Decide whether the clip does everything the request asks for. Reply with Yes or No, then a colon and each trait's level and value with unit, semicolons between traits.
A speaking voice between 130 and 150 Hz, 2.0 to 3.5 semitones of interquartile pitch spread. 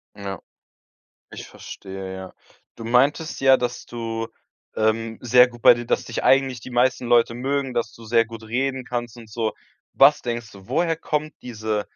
No: low, 120 Hz; narrow, 2.4 semitones